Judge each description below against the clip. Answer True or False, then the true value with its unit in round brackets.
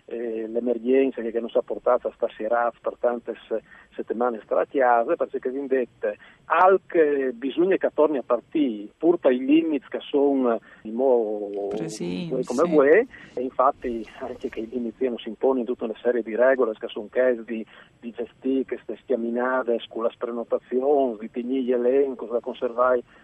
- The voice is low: True (125 Hz)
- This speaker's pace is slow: False (170 wpm)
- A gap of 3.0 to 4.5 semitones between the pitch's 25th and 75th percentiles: False (2.4 semitones)